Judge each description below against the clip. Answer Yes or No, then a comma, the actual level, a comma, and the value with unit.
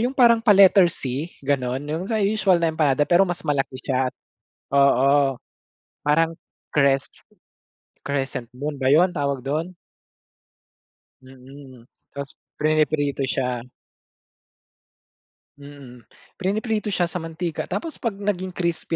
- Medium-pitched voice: Yes, medium, 150 Hz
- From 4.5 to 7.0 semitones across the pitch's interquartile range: Yes, average, 5.0 semitones